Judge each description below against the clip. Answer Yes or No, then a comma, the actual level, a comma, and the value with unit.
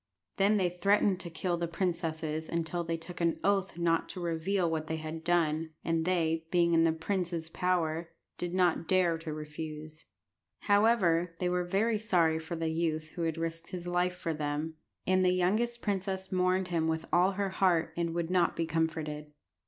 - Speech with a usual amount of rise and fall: No, narrow, 2.2 semitones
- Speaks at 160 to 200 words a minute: Yes, average, 185 wpm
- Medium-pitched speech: Yes, medium, 170 Hz